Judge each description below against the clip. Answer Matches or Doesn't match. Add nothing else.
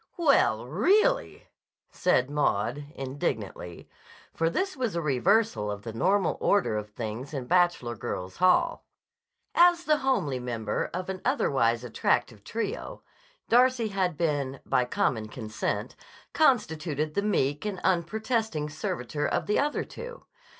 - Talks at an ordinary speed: Doesn't match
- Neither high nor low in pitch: Matches